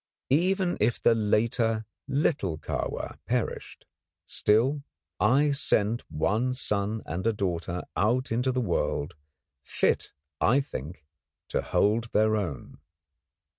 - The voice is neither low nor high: No, low, 110 Hz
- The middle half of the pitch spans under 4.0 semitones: No, average, 4.4 semitones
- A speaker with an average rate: No, slow, 115 wpm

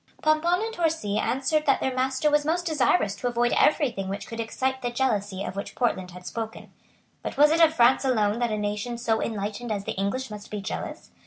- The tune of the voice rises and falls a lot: Yes, wide, 5.8 semitones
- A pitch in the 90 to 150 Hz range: No, high, 240 Hz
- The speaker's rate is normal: No, fast, 220 wpm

